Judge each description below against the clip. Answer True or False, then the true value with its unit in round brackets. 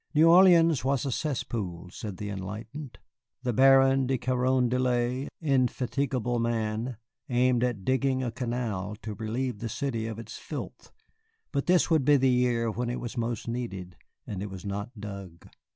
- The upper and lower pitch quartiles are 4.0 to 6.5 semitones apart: False (3.4 semitones)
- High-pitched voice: False (120 Hz)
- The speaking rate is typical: True (160 wpm)